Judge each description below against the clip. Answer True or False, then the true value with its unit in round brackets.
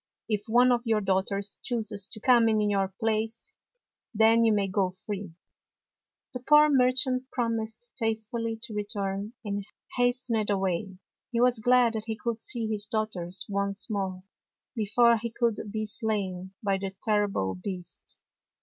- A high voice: True (215 Hz)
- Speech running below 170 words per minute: True (150 wpm)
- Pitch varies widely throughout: False (2.8 semitones)